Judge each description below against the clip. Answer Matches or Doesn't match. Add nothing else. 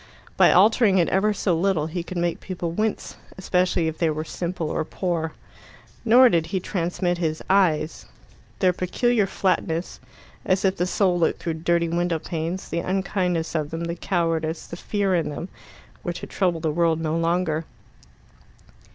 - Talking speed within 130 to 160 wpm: Doesn't match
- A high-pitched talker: Doesn't match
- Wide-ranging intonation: Doesn't match